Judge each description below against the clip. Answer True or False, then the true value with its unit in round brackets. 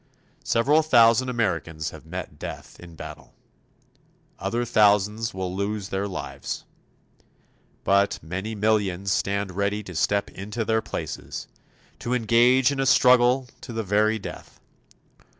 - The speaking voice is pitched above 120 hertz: False (105 Hz)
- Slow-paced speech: True (130 wpm)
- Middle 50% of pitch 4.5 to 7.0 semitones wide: False (3.5 semitones)